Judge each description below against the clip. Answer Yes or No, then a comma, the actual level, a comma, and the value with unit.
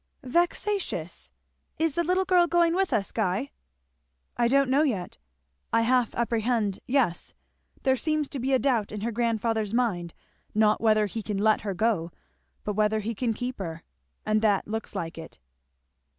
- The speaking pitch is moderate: No, high, 230 Hz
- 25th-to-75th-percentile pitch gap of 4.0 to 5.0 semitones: Yes, average, 4.4 semitones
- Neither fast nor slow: Yes, average, 165 wpm